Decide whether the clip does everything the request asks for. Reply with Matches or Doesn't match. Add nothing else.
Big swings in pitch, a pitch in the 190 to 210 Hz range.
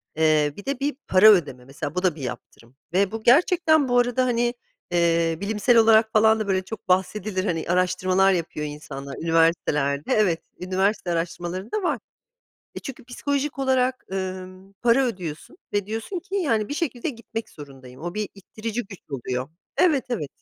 Matches